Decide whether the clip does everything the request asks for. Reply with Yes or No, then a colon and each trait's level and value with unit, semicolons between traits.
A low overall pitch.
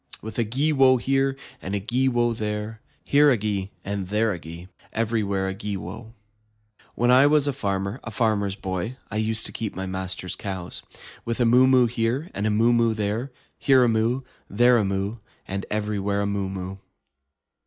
Yes: low, 110 Hz